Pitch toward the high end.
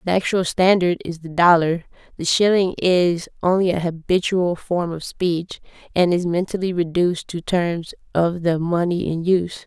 No: medium, 175 Hz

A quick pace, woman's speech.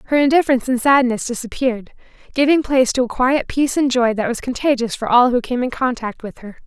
Yes: fast, 215 wpm; female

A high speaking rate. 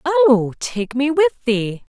No: average, 150 wpm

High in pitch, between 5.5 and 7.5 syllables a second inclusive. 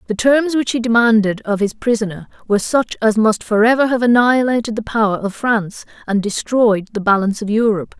Yes: high, 225 Hz; 5.8 syllables/s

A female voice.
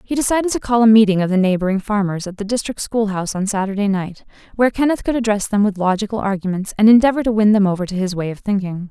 Yes: female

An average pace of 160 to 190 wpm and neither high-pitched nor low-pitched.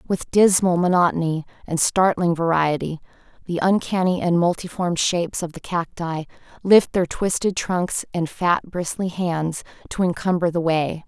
No: average, 140 wpm; medium, 175 Hz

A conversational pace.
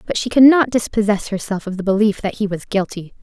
No: fast, 240 wpm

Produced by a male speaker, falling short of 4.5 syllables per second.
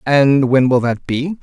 Yes: male; 3.9 syllables/s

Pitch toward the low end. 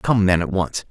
Yes: very low, 95 Hz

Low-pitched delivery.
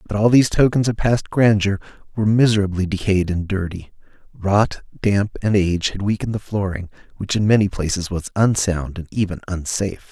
Yes: low, 100 Hz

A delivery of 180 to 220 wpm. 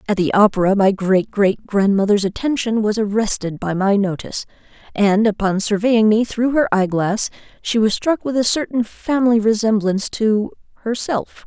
No: average, 160 wpm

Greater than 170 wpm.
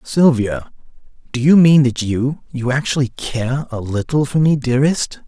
No: average, 150 wpm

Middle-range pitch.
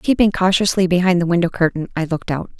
Yes: medium, 180 Hz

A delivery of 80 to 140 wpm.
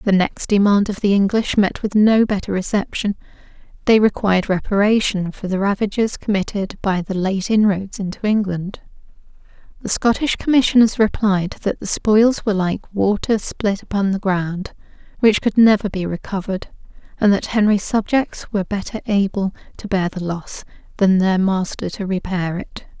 No: average, 155 wpm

